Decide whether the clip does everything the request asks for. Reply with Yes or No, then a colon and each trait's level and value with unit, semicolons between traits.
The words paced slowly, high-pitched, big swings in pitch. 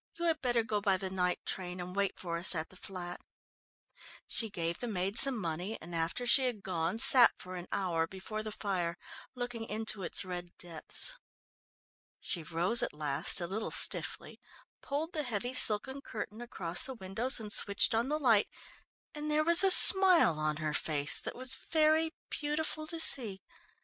No: average, 180 wpm; high, 210 Hz; wide, 6.5 semitones